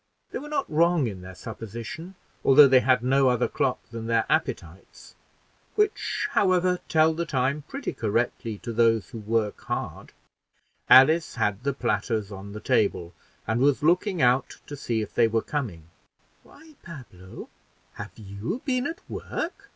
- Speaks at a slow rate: No, average, 160 wpm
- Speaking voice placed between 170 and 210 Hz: No, low, 125 Hz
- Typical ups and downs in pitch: No, wide, 6.9 semitones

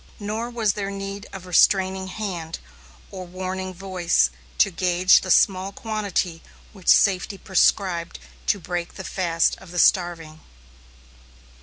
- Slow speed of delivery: Yes, slow, 130 wpm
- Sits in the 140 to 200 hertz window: Yes, medium, 185 Hz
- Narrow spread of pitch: Yes, narrow, 2.0 semitones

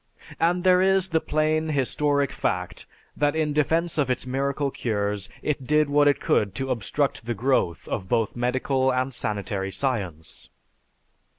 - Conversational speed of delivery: Yes, average, 155 wpm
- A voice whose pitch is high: No, low, 135 Hz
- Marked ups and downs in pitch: No, average, 4.8 semitones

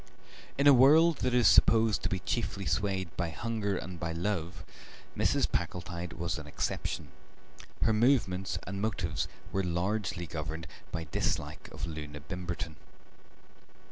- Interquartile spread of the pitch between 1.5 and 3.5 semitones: No, average, 4.6 semitones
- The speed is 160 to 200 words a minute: No, average, 140 wpm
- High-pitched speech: No, very low, 95 Hz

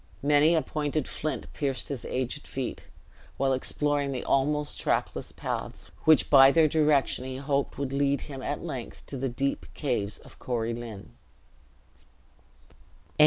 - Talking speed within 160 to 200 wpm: No, average, 145 wpm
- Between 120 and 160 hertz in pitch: Yes, medium, 140 Hz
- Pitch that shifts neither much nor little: No, narrow, 2.1 semitones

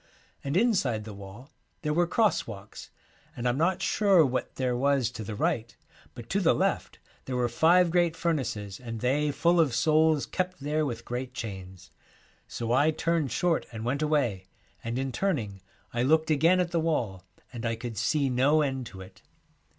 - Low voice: Yes, low, 130 Hz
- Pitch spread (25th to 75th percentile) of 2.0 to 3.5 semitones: No, wide, 5.6 semitones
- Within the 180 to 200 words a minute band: Yes, average, 190 wpm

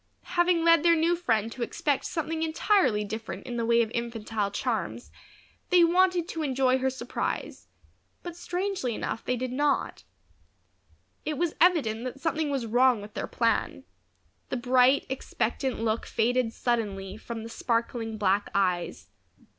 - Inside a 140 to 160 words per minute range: Yes, average, 150 wpm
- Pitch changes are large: Yes, wide, 6.1 semitones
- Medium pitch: No, very high, 250 Hz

